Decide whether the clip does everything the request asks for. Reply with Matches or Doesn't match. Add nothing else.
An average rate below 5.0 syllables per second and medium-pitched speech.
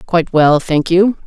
Matches